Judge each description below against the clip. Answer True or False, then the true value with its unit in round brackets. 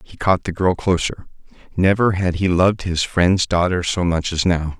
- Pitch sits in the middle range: False (90 Hz)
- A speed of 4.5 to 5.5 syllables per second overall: True (4.8 syllables/s)